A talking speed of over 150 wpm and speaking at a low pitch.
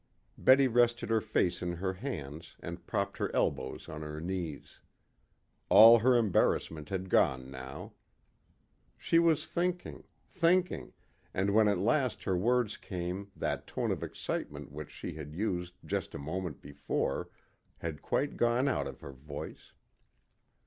No: average, 145 wpm; very low, 95 Hz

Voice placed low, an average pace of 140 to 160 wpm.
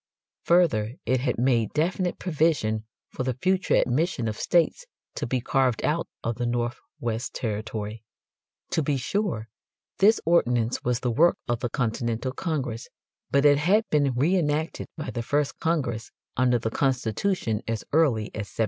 Yes: low, 130 Hz; average, 155 wpm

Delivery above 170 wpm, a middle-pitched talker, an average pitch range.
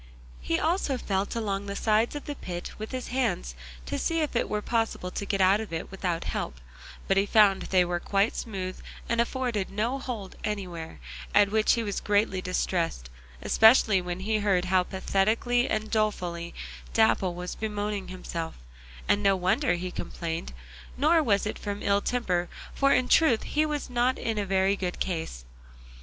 No: average, 180 wpm; high, 200 Hz; average, 3.7 semitones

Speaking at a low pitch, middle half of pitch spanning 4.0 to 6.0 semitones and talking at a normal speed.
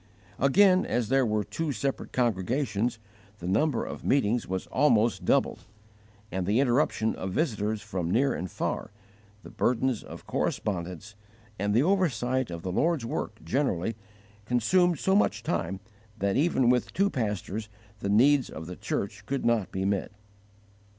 Yes: low, 115 Hz; wide, 5.4 semitones; average, 150 wpm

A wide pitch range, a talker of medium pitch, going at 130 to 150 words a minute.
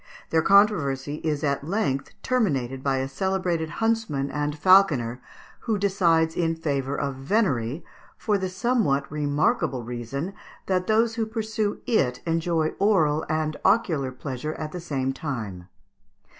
Yes: wide, 6.1 semitones; medium, 155 Hz; slow, 135 wpm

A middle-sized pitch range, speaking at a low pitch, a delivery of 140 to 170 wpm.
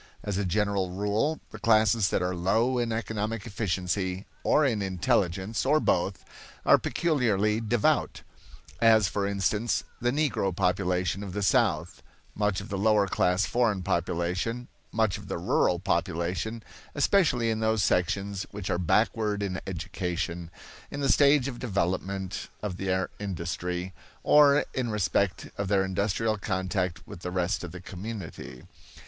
Yes: average, 3.5 semitones; low, 100 Hz; average, 145 wpm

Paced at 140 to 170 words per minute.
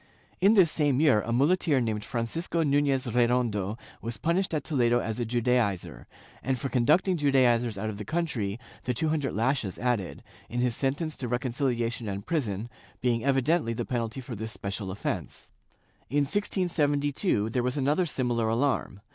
Yes: average, 165 wpm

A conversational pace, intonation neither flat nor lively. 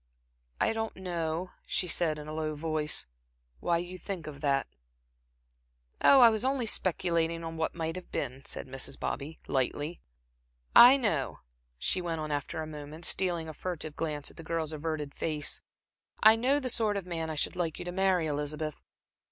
Yes: average, 180 wpm; average, 3.2 semitones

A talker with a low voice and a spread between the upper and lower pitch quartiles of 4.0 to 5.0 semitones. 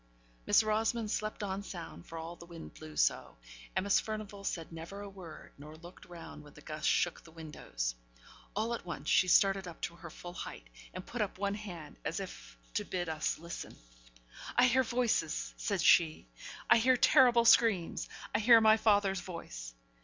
No: medium, 185 Hz; average, 4.6 semitones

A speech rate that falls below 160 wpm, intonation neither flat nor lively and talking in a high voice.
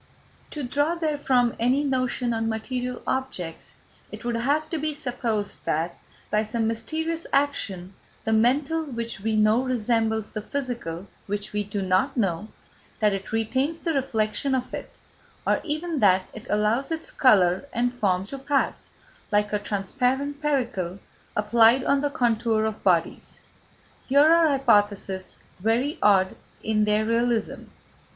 Yes: average, 145 wpm; average, 4.7 semitones; high, 230 Hz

